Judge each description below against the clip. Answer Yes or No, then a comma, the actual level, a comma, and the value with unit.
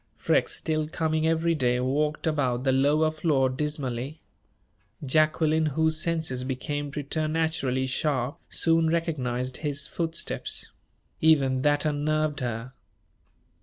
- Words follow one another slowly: Yes, slow, 110 wpm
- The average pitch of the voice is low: No, medium, 150 Hz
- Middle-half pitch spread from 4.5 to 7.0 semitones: No, average, 3.2 semitones